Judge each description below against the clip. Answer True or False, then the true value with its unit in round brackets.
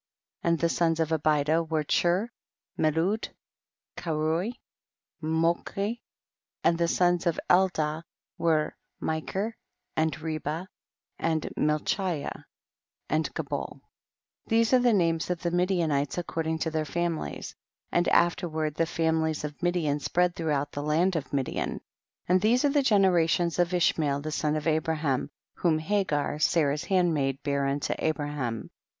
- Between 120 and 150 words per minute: True (140 wpm)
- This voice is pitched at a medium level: True (160 Hz)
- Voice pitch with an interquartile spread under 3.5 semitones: True (2.6 semitones)